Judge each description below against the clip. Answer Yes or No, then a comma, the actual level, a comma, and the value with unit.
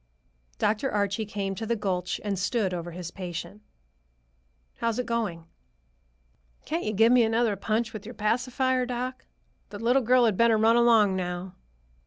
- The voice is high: Yes, high, 220 Hz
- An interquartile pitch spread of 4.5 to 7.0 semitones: No, average, 3.5 semitones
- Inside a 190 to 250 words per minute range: No, average, 160 wpm